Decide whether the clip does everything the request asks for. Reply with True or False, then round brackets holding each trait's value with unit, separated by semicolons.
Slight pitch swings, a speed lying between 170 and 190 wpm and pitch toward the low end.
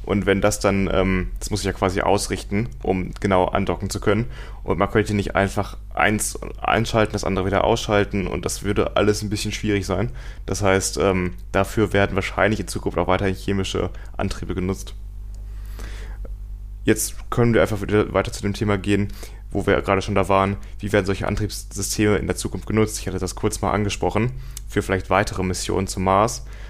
True (1.6 semitones; 185 wpm; 100 Hz)